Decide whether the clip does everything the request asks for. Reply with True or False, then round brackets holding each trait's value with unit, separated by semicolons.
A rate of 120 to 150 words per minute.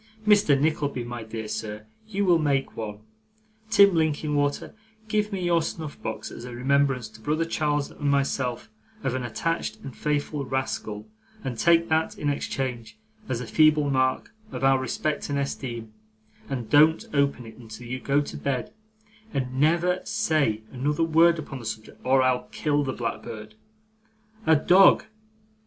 False (160 wpm)